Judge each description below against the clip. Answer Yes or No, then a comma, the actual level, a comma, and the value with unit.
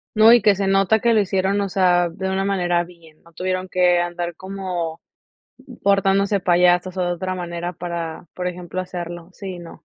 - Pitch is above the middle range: No, medium, 180 Hz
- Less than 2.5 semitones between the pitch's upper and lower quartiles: Yes, narrow, 1.9 semitones